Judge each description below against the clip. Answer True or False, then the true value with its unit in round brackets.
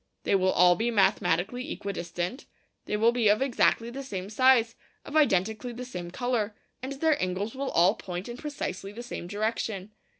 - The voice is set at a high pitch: True (220 Hz)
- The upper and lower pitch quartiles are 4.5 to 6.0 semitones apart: True (5.0 semitones)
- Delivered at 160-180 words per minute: True (175 wpm)